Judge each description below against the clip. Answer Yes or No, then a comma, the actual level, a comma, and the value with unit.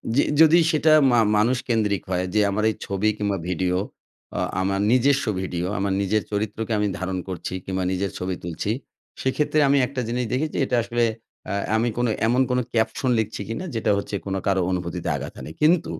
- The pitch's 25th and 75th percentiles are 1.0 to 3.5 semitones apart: No, average, 4.8 semitones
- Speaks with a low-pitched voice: Yes, low, 110 Hz